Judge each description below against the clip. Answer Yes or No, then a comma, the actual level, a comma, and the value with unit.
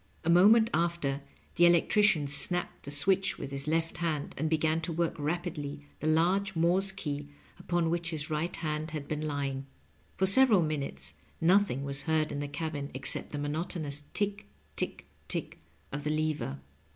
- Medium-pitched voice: Yes, medium, 160 Hz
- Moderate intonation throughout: Yes, average, 3.1 semitones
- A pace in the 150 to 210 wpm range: Yes, average, 170 wpm